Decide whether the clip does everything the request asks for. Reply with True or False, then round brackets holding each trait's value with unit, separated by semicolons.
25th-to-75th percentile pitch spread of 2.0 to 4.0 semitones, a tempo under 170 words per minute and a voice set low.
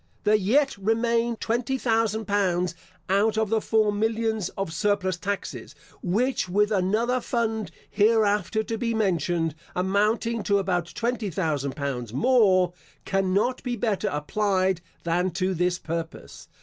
False (3.7 semitones; 135 wpm; 205 Hz)